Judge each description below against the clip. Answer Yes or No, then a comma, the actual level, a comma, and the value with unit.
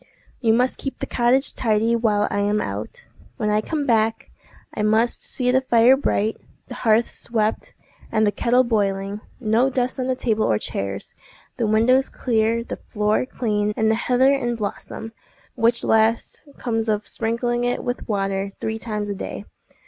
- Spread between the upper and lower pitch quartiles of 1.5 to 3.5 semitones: Yes, narrow, 2.5 semitones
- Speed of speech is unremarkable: Yes, average, 170 wpm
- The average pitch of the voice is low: No, high, 225 Hz